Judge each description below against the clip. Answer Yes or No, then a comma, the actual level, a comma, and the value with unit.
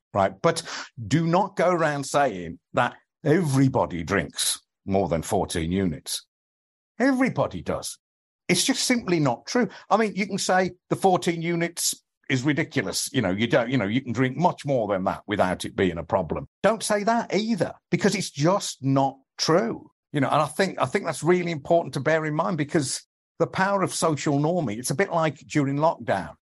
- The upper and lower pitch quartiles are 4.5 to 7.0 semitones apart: Yes, average, 5.1 semitones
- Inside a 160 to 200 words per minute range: Yes, average, 190 wpm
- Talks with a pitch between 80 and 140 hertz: No, medium, 160 Hz